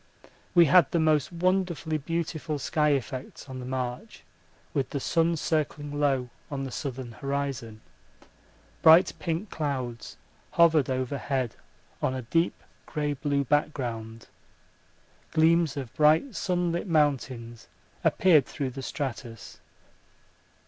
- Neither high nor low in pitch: Yes, medium, 145 Hz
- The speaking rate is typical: No, slow, 115 wpm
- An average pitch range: Yes, average, 3.9 semitones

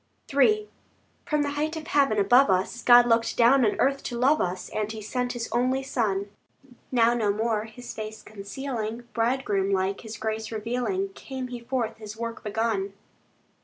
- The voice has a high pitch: Yes, high, 230 Hz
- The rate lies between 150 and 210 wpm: Yes, average, 170 wpm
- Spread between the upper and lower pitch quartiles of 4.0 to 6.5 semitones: No, average, 3.5 semitones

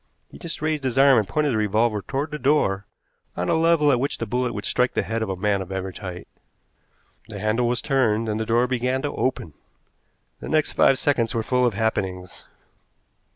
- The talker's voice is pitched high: No, low, 115 Hz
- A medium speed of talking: No, fast, 210 wpm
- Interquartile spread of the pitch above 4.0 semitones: Yes, average, 4.4 semitones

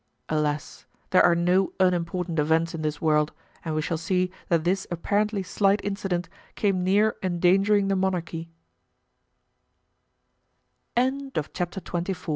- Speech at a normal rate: No, slow, 120 wpm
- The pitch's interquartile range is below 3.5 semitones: Yes, average, 2.9 semitones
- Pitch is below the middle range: No, medium, 180 Hz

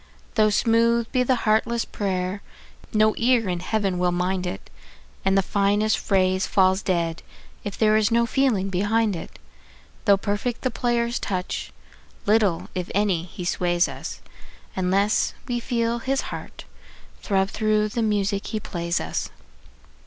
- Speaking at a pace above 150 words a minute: No, average, 145 wpm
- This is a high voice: Yes, high, 205 Hz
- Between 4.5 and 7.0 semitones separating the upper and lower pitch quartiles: No, average, 3.4 semitones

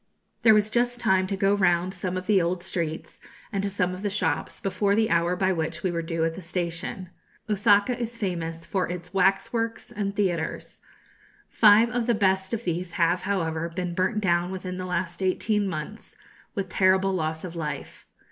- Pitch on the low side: No, medium, 185 Hz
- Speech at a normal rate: Yes, average, 195 wpm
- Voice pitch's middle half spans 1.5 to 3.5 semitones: Yes, average, 2.9 semitones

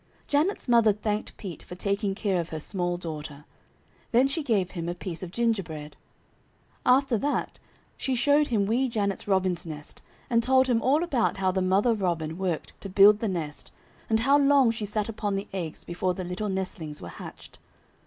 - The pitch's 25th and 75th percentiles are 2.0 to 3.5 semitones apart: No, average, 4.8 semitones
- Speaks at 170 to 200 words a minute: Yes, average, 185 wpm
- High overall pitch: Yes, high, 200 Hz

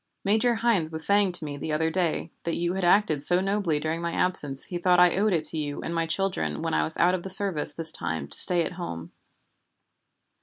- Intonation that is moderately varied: Yes, average, 3.3 semitones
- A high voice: No, medium, 170 Hz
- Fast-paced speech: Yes, fast, 235 wpm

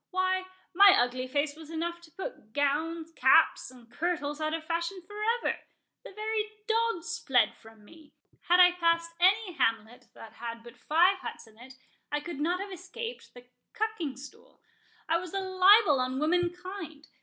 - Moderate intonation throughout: Yes, average, 4.7 semitones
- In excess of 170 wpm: No, average, 160 wpm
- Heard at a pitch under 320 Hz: No, very high, 335 Hz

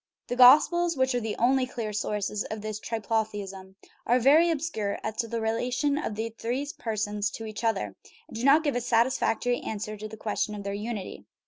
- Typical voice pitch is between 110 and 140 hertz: No, high, 225 Hz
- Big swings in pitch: No, average, 3.0 semitones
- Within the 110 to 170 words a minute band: No, average, 200 wpm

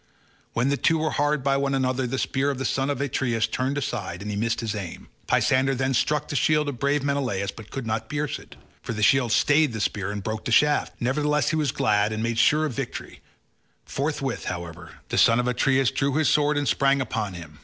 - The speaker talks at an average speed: No, fast, 230 wpm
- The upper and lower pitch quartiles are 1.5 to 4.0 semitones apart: No, average, 4.4 semitones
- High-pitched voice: No, low, 130 Hz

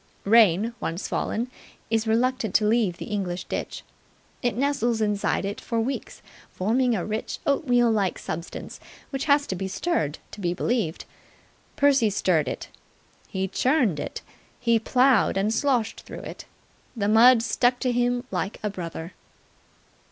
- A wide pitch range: No, average, 4.2 semitones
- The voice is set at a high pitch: Yes, high, 225 Hz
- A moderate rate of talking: Yes, average, 150 wpm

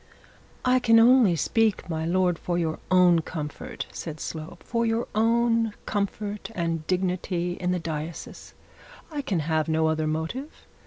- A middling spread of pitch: No, wide, 5.7 semitones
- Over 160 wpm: No, average, 145 wpm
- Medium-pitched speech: Yes, medium, 180 Hz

